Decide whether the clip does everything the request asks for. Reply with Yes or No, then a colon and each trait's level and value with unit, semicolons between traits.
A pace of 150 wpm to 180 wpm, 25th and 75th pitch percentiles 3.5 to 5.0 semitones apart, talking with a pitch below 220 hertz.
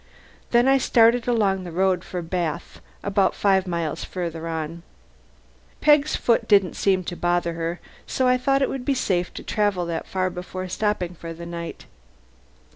Yes: average, 170 wpm; average, 4.5 semitones; medium, 185 Hz